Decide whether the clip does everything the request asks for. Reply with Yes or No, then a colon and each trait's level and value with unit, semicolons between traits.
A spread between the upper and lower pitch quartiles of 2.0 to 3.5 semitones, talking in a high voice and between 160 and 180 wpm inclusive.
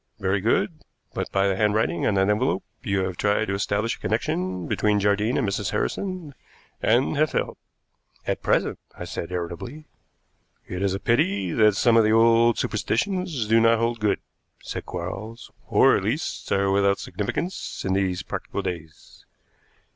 No: average, 3.1 semitones; low, 105 Hz; average, 165 wpm